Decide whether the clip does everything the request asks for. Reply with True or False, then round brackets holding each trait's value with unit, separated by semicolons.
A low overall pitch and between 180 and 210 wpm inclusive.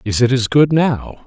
False (130 Hz; 235 wpm)